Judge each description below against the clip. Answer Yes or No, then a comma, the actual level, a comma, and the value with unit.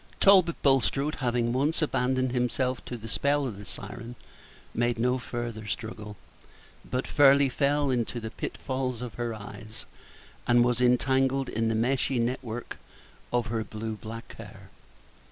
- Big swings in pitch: No, narrow, 2.6 semitones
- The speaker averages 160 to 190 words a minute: No, average, 150 wpm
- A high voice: No, low, 125 Hz